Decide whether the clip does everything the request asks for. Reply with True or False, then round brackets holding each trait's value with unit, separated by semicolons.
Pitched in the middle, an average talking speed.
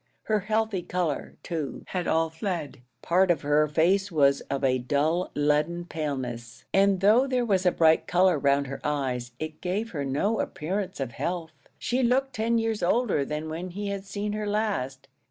True (175 Hz; 180 wpm)